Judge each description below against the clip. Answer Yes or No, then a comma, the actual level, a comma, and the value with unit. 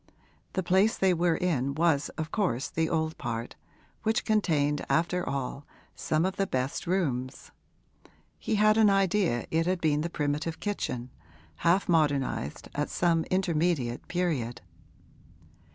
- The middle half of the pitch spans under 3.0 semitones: No, average, 4.5 semitones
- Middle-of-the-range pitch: Yes, medium, 165 Hz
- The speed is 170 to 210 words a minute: No, average, 140 wpm